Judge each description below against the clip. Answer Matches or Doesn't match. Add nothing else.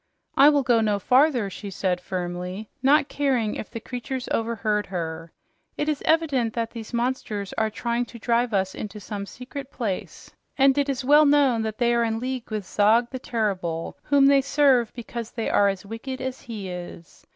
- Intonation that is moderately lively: Matches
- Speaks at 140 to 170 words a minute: Doesn't match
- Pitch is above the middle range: Matches